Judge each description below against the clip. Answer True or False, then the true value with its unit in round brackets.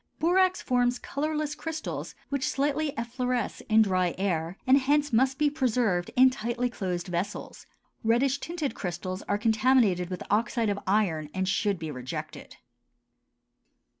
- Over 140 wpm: False (135 wpm)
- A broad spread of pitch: True (6.5 semitones)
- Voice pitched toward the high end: True (235 Hz)